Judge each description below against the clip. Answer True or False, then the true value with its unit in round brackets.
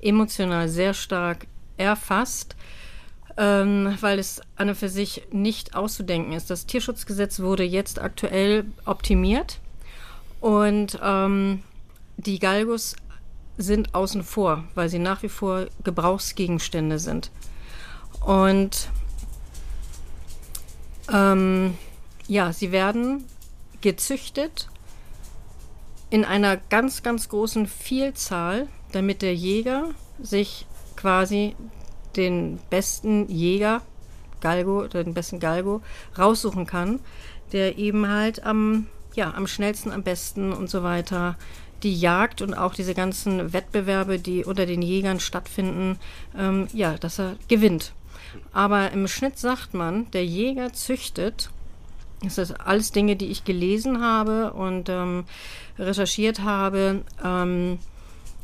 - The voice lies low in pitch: False (195 Hz)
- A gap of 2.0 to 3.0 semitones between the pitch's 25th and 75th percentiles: True (2.5 semitones)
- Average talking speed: False (115 wpm)